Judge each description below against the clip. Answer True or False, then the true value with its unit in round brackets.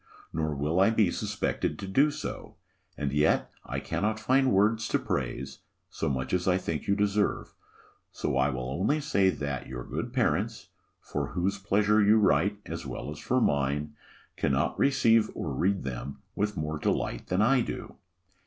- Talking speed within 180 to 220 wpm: False (170 wpm)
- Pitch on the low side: True (95 Hz)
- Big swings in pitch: True (6.9 semitones)